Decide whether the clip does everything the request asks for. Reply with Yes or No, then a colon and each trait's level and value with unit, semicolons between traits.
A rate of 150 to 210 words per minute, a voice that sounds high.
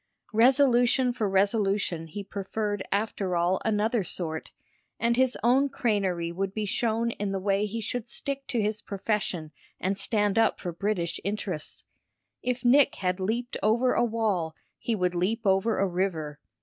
Yes: average, 160 wpm; high, 205 Hz